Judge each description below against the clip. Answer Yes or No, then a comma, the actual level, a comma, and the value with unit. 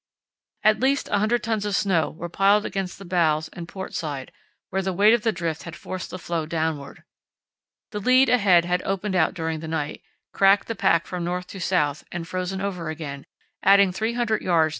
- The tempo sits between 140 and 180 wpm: No, average, 195 wpm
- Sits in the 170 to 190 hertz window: Yes, medium, 185 Hz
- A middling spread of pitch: Yes, average, 3.7 semitones